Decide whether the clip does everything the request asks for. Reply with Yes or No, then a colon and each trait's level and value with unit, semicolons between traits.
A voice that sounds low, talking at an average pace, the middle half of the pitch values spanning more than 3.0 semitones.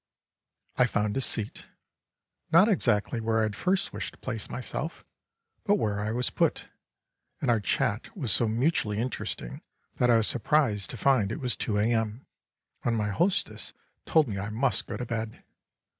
Yes: low, 115 Hz; average, 175 wpm; average, 3.7 semitones